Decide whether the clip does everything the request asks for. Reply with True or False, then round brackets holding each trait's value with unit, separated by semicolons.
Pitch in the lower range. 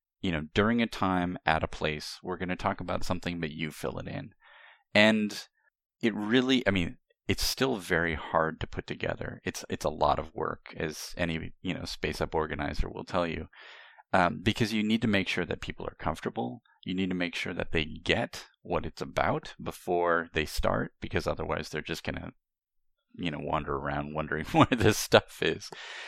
True (85 Hz)